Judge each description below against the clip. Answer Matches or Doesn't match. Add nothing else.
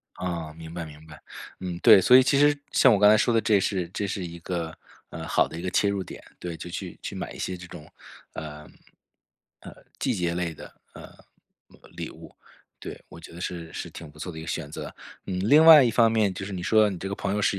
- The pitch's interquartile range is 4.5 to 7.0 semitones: Doesn't match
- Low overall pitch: Matches